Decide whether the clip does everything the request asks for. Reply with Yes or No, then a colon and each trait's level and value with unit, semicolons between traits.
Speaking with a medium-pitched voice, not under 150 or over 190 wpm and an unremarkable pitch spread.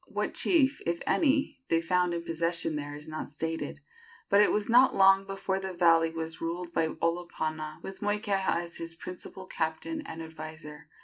Yes: medium, 170 Hz; average, 175 wpm; average, 3.1 semitones